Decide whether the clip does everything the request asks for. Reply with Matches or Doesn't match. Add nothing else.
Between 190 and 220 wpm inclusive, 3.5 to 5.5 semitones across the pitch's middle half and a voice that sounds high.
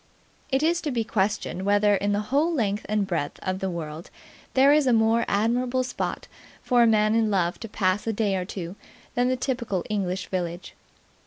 Matches